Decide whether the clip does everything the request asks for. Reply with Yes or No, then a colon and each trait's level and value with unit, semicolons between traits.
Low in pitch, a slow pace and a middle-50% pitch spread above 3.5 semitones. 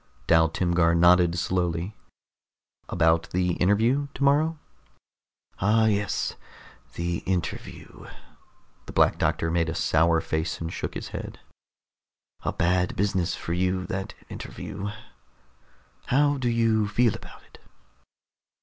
Yes: very low, 90 Hz; slow, 115 wpm; average, 4.3 semitones